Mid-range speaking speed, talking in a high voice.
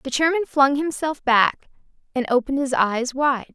Yes: average, 170 wpm; very high, 270 Hz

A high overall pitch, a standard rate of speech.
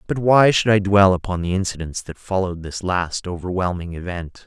No: very low, 95 Hz; average, 190 wpm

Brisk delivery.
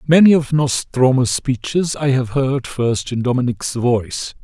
No: average, 150 wpm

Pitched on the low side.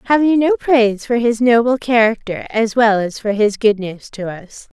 No: high, 225 Hz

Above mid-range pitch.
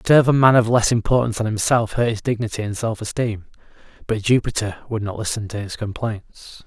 No: low, 110 Hz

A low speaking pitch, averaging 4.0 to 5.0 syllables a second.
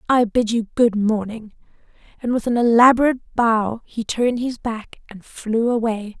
No: high, 230 Hz; 4.8 syllables/s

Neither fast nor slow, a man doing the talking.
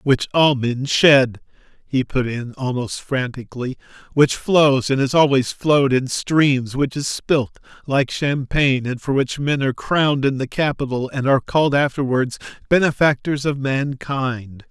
Yes: average, 155 wpm; male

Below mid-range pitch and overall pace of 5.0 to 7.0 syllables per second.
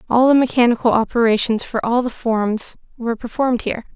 No: high, 235 Hz; 6.1 syllables/s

